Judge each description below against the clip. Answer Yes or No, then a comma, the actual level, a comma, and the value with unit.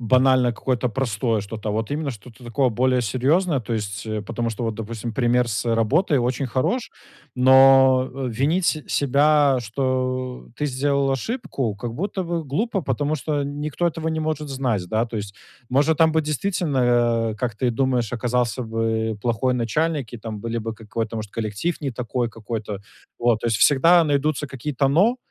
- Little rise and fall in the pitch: No, average, 4.1 semitones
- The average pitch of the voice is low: Yes, low, 125 Hz